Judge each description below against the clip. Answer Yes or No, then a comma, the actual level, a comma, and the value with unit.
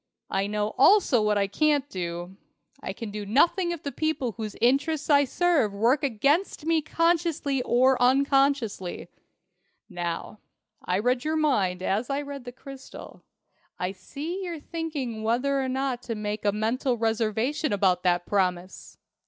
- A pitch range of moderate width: No, wide, 5.7 semitones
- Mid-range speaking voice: No, very high, 250 Hz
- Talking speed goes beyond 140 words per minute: Yes, average, 155 wpm